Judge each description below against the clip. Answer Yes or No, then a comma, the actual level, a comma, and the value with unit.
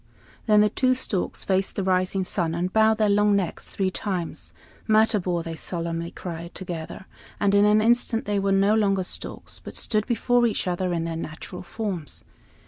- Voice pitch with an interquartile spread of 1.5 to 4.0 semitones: Yes, average, 3.3 semitones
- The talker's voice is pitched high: Yes, high, 195 Hz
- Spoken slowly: No, average, 180 wpm